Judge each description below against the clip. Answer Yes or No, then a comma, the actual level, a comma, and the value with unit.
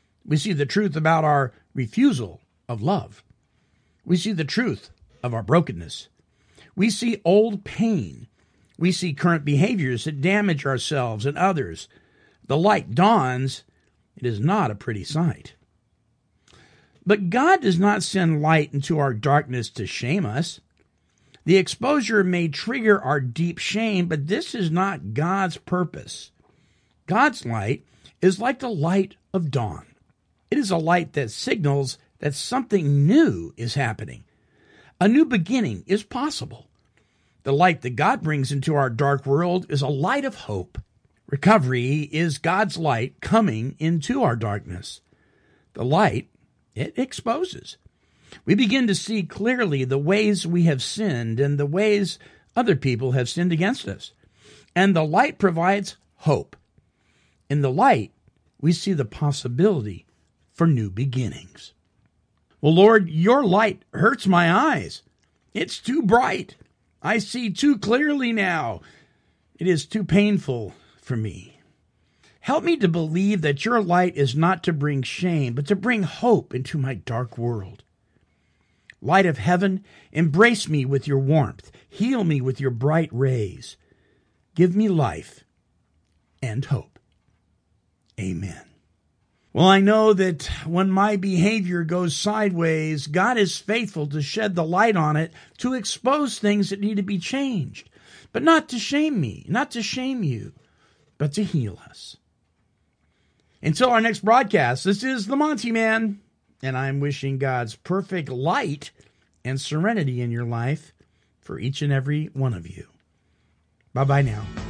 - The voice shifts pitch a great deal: Yes, wide, 7.5 semitones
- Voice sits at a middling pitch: Yes, medium, 160 Hz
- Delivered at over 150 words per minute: No, average, 145 wpm